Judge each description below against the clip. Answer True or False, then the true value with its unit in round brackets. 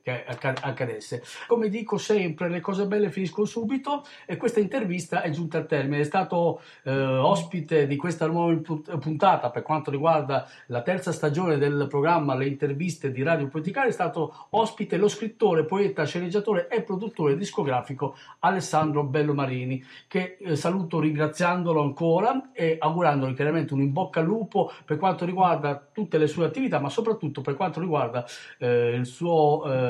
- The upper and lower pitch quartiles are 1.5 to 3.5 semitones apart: False (4.7 semitones)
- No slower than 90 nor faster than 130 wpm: False (160 wpm)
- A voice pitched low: False (160 Hz)